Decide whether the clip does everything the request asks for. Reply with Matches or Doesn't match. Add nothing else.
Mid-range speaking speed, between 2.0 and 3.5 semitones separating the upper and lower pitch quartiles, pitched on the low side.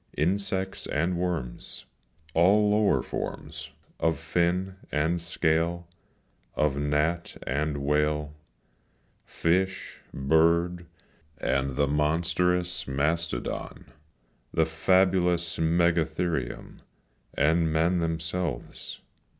Doesn't match